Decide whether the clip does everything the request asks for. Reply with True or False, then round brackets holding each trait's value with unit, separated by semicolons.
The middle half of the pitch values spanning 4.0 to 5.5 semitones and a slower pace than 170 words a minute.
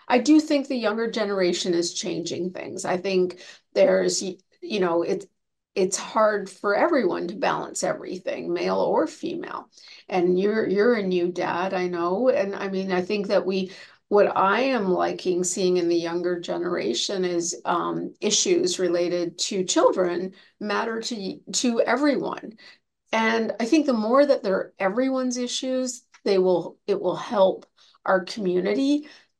True (4.5 semitones; 155 wpm)